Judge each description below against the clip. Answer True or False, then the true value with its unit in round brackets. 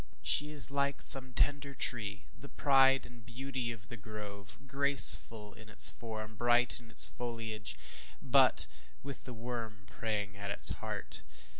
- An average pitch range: True (3.8 semitones)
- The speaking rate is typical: True (150 wpm)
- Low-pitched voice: True (115 Hz)